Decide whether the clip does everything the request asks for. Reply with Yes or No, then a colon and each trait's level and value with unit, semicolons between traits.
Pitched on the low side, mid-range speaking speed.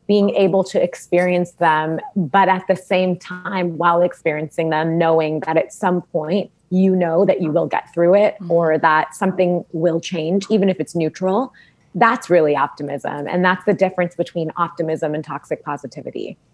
No: medium, 175 Hz; average, 170 wpm